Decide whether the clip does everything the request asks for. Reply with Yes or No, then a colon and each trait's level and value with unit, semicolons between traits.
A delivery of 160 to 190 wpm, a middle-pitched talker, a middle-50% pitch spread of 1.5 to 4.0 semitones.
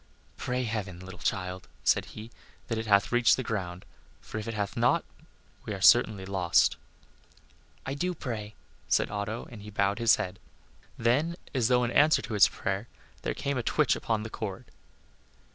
No: average, 180 wpm; low, 110 Hz; average, 3.4 semitones